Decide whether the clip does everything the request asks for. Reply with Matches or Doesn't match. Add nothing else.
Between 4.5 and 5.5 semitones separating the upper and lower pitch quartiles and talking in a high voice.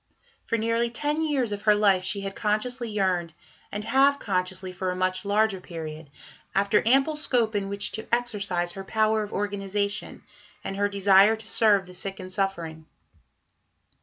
Doesn't match